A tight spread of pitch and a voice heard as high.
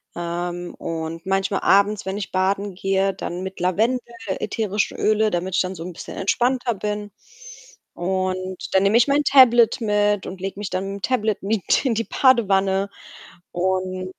Yes: narrow, 2.3 semitones; high, 195 Hz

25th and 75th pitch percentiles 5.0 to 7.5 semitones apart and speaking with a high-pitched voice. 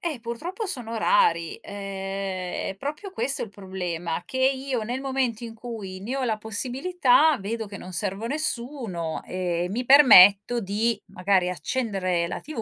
Yes: wide, 5.6 semitones; high, 225 Hz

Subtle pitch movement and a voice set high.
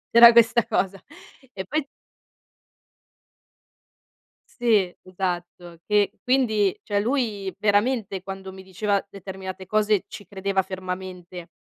Yes: narrow, 2.3 semitones; high, 195 Hz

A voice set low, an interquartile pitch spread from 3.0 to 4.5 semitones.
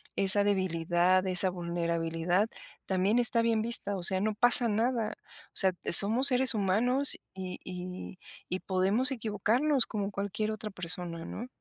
No: high, 200 Hz; average, 3.7 semitones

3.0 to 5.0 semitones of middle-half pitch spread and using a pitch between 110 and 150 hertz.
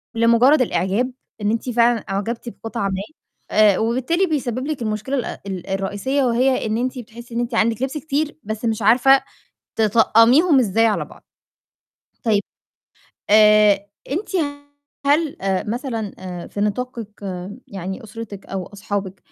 No: average, 3.7 semitones; high, 225 Hz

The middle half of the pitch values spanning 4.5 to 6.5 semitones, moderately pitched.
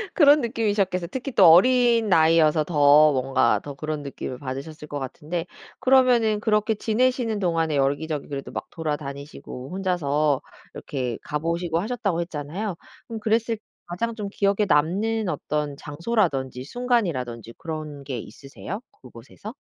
No: wide, 7.0 semitones; medium, 165 Hz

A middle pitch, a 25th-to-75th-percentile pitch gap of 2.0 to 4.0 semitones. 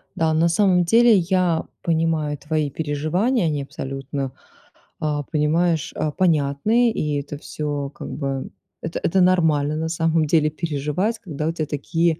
Yes: medium, 160 Hz; average, 2.7 semitones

